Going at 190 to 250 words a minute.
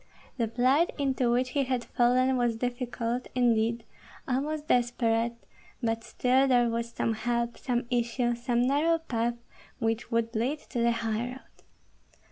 No: average, 140 wpm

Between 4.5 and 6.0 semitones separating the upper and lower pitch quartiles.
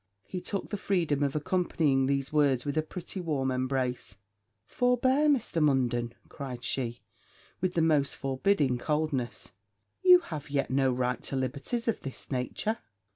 Yes: average, 5.3 semitones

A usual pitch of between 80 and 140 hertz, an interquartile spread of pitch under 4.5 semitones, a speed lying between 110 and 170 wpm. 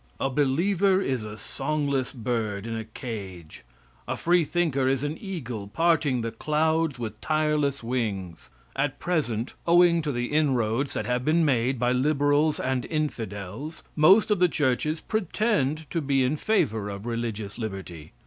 No: low, 135 Hz; average, 5.2 semitones; average, 150 wpm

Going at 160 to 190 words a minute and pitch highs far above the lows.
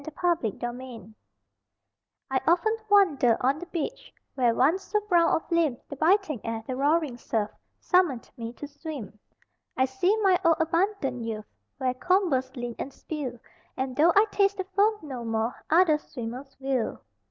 Yes: average, 165 wpm; wide, 6.1 semitones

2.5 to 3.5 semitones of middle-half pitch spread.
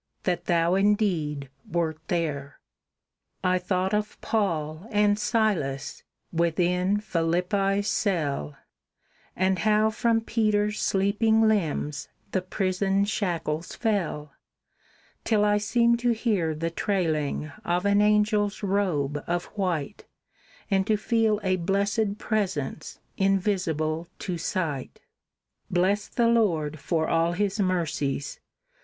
No: average, 4.1 semitones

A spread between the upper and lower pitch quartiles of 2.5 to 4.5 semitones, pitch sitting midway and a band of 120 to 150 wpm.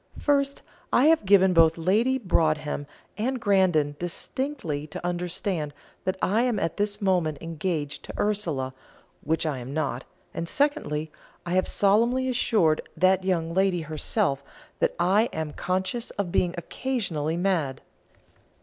No: average, 4.9 semitones; medium, 180 Hz; average, 140 wpm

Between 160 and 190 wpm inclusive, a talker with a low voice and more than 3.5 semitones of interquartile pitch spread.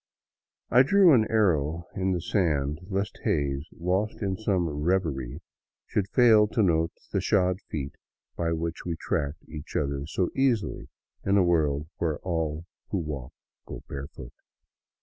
No: average, 150 wpm; very low, 85 Hz; average, 4.8 semitones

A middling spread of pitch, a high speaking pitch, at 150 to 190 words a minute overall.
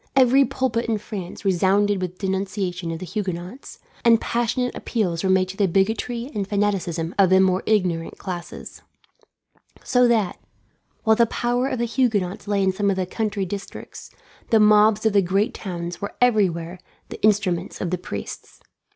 Yes: average, 3.3 semitones; high, 200 Hz; average, 170 wpm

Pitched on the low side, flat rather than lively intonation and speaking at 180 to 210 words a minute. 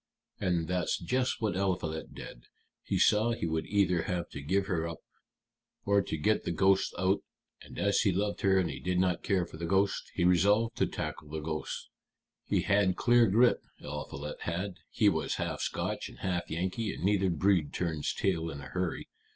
No: very low, 90 Hz; average, 3.2 semitones; average, 190 wpm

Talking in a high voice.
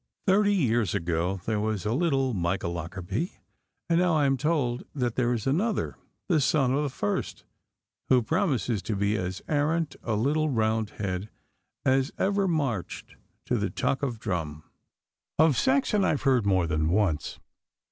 No: low, 125 Hz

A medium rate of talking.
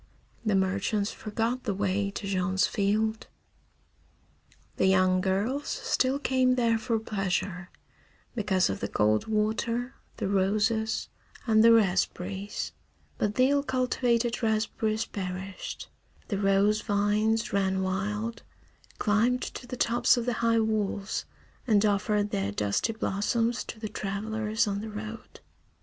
No: slow, 130 wpm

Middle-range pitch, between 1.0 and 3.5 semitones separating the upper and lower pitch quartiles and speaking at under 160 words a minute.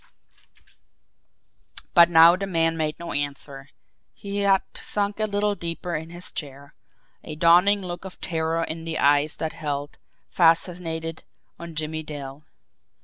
Yes: medium, 165 Hz; narrow, 2.6 semitones; average, 140 wpm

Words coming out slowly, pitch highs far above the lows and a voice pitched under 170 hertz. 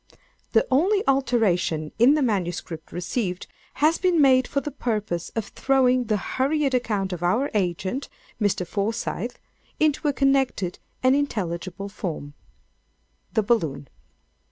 No: slow, 130 wpm; wide, 6.7 semitones; high, 230 Hz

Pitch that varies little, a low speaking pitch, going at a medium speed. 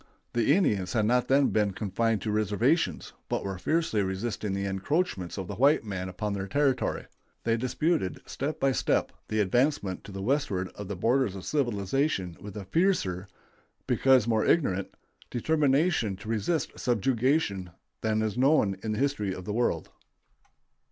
No: wide, 5.6 semitones; low, 110 Hz; average, 160 wpm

